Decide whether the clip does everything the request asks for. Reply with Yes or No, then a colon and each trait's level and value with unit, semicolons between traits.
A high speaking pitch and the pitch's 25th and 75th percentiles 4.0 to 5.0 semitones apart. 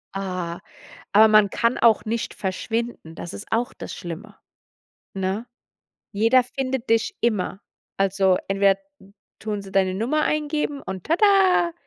Yes: high, 215 Hz; average, 4.6 semitones